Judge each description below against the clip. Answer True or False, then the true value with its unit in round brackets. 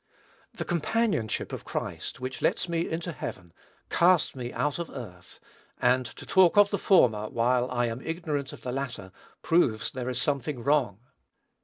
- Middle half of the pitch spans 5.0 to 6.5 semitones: True (5.6 semitones)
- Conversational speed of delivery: True (165 wpm)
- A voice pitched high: False (130 Hz)